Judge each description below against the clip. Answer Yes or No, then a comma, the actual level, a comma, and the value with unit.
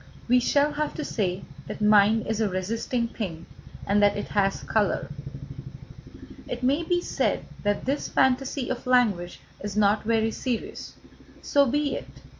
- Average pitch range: Yes, average, 4.2 semitones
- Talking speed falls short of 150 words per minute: No, average, 155 wpm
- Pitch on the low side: No, high, 225 Hz